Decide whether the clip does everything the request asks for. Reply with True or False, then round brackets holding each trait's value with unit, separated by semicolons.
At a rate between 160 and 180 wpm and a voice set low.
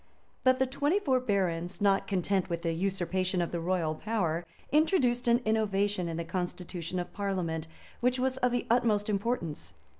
False (170 wpm; 195 Hz)